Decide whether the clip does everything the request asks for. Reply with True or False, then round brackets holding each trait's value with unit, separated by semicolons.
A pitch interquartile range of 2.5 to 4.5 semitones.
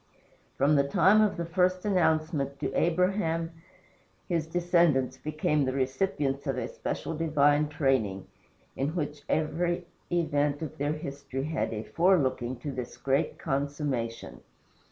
True (3.5 semitones)